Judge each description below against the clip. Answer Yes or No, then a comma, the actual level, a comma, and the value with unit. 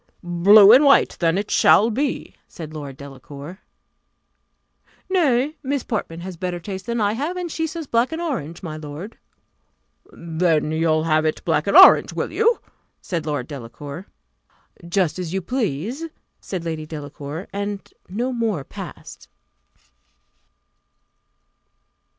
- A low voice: No, medium, 180 Hz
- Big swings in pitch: Yes, wide, 7.1 semitones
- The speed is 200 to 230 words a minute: No, average, 140 wpm